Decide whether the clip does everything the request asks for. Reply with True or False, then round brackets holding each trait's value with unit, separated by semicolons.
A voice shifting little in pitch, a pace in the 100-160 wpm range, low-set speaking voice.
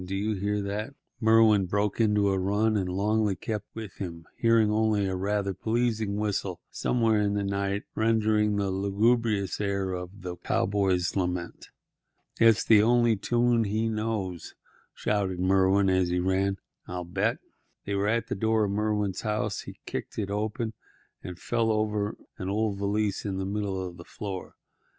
False (2.1 semitones; 170 wpm; 100 Hz)